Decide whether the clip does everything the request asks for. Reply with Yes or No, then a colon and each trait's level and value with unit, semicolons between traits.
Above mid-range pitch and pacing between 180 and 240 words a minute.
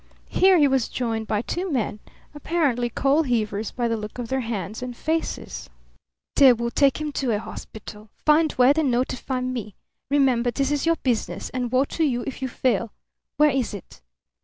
Yes: very high, 255 Hz; average, 185 wpm